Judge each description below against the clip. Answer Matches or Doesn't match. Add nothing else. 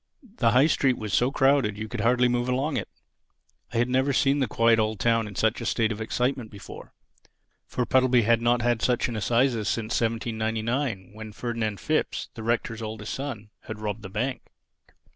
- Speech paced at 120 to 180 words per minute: Doesn't match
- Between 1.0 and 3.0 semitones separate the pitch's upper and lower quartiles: Matches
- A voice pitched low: Matches